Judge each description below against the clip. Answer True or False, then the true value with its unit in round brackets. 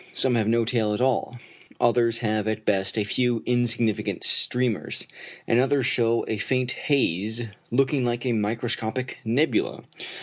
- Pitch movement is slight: True (2.3 semitones)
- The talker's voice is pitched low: True (115 Hz)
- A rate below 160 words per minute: True (145 wpm)